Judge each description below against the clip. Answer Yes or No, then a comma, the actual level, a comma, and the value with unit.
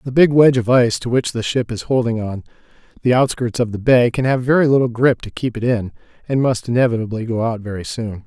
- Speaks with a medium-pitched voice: No, low, 120 Hz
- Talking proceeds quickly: Yes, fast, 240 wpm